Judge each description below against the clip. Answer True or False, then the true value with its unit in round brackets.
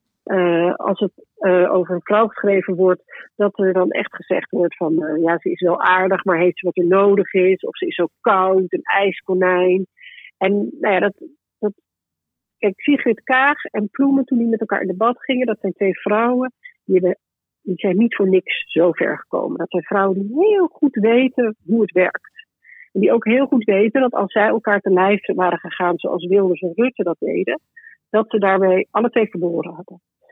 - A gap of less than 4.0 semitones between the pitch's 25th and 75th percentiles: False (4.3 semitones)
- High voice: True (195 Hz)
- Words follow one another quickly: True (205 wpm)